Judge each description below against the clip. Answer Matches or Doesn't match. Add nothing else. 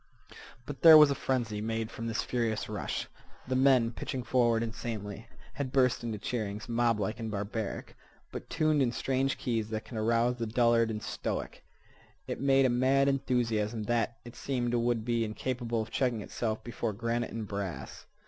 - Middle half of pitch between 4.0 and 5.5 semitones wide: Doesn't match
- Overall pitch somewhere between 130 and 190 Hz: Doesn't match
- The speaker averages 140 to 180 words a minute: Matches